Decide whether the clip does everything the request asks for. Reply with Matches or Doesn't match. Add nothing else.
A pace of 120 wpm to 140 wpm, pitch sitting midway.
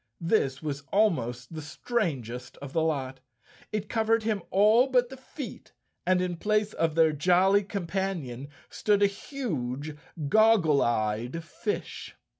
Matches